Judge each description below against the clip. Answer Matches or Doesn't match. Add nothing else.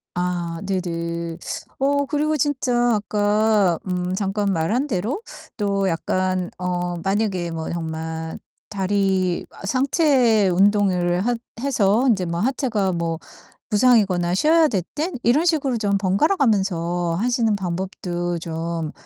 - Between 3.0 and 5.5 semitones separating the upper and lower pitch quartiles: Matches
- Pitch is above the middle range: Matches